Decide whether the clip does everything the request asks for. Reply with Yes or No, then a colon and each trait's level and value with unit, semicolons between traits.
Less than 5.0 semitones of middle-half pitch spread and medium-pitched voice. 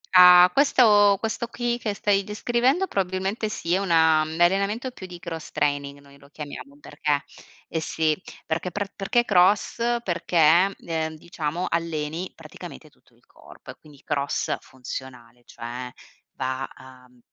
No: wide, 5.5 semitones; medium, 170 Hz